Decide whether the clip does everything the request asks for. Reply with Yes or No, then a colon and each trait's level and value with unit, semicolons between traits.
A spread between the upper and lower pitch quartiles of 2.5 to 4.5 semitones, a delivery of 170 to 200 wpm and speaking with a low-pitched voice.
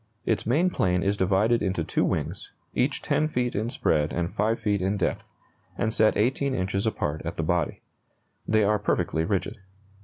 Yes: average, 3.8 semitones; average, 180 wpm; low, 105 Hz